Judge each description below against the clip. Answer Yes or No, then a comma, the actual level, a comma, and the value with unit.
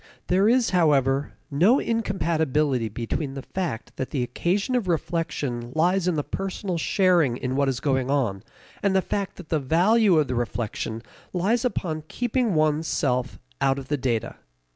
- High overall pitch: No, medium, 155 Hz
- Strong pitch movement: Yes, wide, 6.1 semitones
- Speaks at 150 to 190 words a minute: Yes, average, 165 wpm